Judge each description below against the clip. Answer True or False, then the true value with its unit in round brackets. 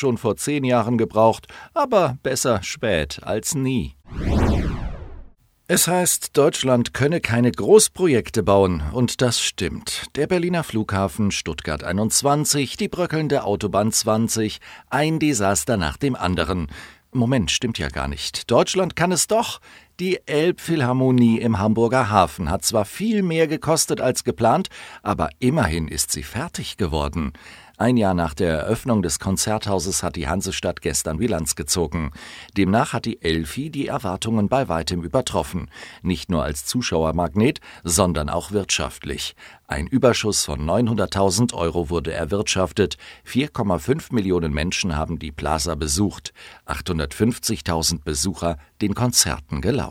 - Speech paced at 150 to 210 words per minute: False (130 wpm)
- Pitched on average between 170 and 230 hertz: False (105 Hz)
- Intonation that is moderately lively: False (7.0 semitones)